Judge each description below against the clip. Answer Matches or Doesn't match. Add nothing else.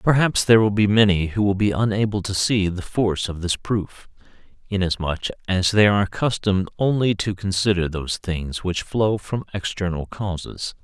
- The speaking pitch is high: Doesn't match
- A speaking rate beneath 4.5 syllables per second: Doesn't match